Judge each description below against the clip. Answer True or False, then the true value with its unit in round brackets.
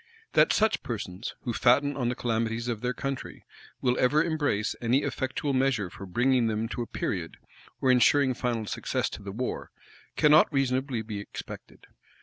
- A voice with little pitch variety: False (3.2 semitones)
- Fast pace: False (165 wpm)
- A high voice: False (125 Hz)